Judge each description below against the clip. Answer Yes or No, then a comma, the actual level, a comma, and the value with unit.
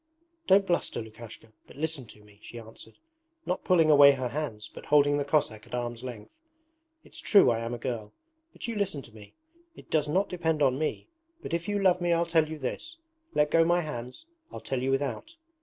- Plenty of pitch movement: Yes, wide, 6.0 semitones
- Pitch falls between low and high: Yes, medium, 145 Hz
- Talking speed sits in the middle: No, fast, 210 wpm